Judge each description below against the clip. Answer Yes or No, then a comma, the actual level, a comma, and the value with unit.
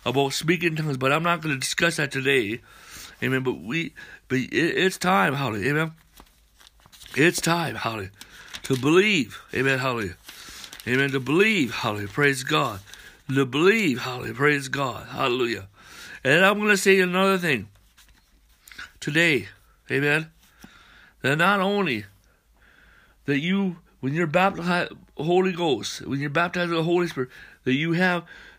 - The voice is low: No, medium, 145 Hz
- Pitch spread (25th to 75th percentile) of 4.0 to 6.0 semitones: Yes, average, 5.2 semitones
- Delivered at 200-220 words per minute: No, average, 145 wpm